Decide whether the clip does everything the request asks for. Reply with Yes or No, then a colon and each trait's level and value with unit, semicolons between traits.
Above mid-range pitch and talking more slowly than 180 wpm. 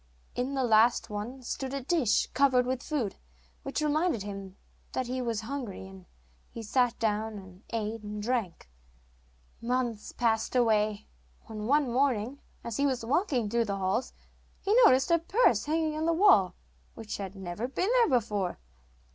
Yes: high, 235 Hz; average, 165 wpm